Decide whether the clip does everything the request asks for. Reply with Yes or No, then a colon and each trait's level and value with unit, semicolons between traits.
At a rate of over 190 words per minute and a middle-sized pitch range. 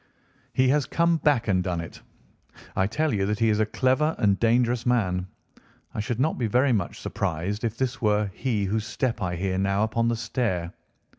Yes: average, 200 wpm; average, 4.3 semitones